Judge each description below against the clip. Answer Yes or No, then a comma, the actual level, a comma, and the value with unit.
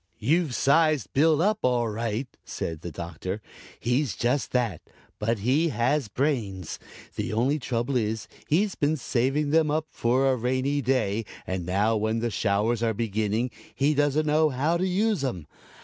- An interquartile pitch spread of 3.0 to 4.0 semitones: No, average, 5.2 semitones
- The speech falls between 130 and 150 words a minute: No, average, 165 wpm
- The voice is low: Yes, low, 125 Hz